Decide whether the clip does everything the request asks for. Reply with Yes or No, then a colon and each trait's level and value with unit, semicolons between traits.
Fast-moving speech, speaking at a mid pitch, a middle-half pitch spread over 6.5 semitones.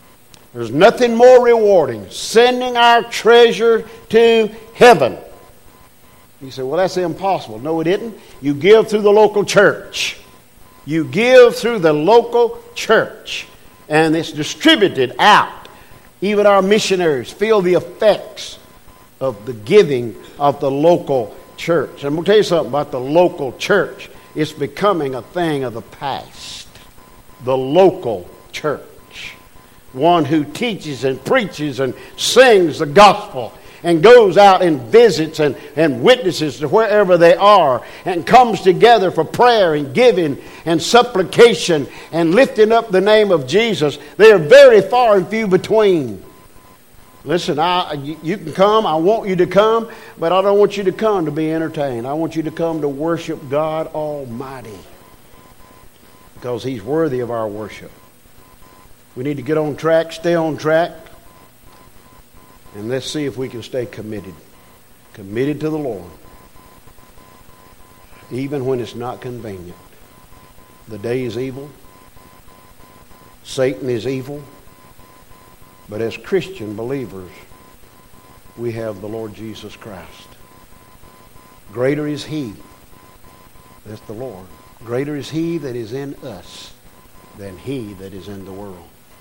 No: average, 140 wpm; medium, 155 Hz; wide, 8.1 semitones